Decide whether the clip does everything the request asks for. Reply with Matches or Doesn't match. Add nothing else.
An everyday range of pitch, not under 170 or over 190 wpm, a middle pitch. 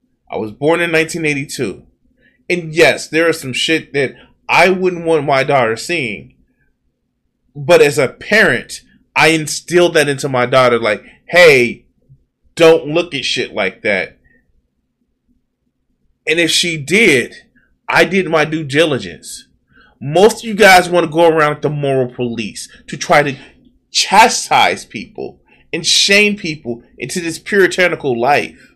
Doesn't match